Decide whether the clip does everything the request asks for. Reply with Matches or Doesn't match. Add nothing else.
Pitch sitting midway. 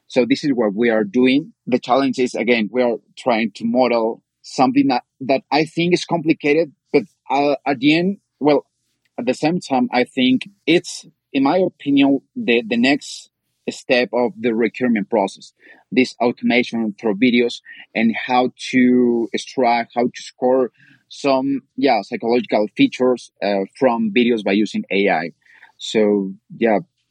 Doesn't match